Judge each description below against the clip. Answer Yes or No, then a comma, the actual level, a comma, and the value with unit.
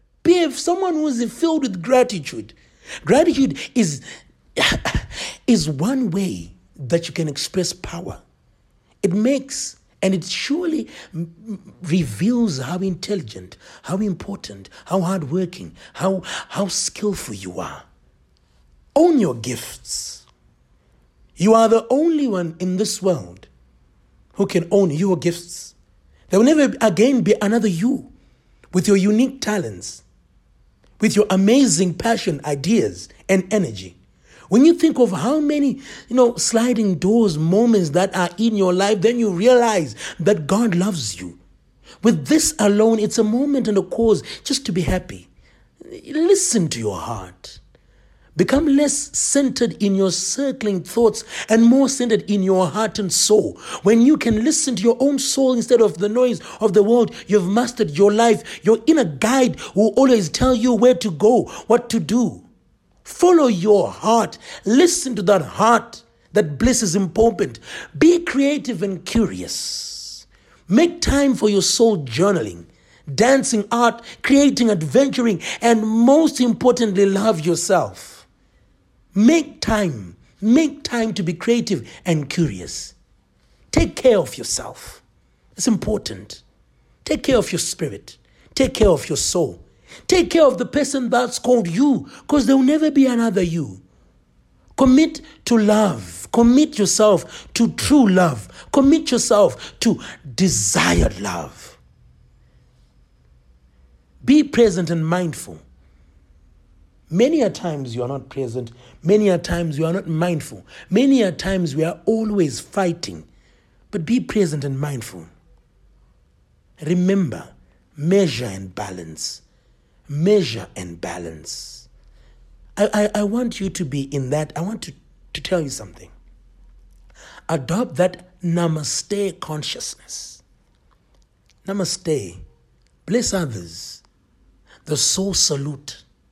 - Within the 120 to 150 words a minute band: Yes, slow, 135 wpm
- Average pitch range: No, wide, 7.8 semitones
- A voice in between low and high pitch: No, high, 200 Hz